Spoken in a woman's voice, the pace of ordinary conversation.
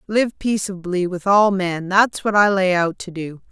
Yes: female; average, 190 wpm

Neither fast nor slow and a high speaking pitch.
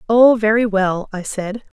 Yes: average, 170 wpm; high, 210 Hz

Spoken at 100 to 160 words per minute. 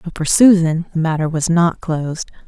No: average, 195 wpm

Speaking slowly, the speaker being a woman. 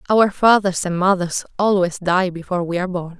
No: average, 190 wpm; female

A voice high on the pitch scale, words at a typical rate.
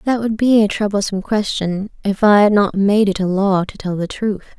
No: high, 200 Hz; fast, 235 wpm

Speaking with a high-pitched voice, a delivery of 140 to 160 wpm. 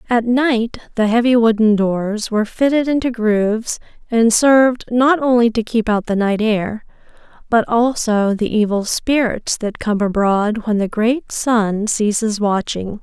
Yes: high, 225 Hz; average, 155 wpm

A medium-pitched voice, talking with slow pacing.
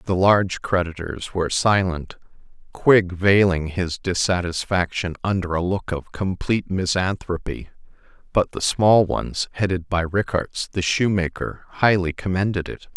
No: very low, 90 Hz; slow, 115 wpm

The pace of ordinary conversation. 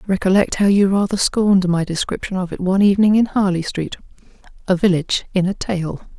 Yes: average, 185 wpm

